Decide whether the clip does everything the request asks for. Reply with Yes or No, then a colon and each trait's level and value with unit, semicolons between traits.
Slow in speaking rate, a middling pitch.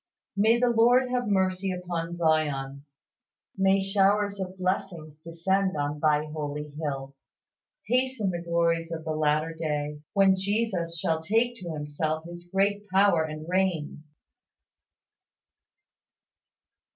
Yes: slow, 120 wpm; medium, 175 Hz